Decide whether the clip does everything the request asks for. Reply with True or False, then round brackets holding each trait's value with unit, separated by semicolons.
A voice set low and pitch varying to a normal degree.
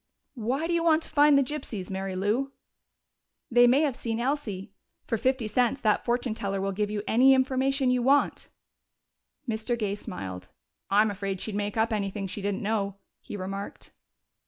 False (220 Hz; 4.7 semitones)